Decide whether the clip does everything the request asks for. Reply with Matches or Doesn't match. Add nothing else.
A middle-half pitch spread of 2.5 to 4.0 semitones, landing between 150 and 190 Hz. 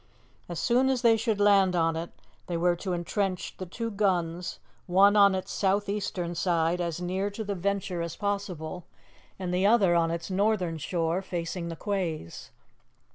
Matches